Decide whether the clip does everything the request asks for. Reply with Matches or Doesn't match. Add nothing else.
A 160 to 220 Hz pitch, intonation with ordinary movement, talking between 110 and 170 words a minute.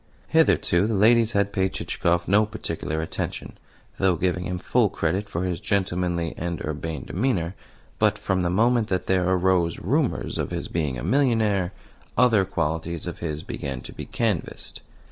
Doesn't match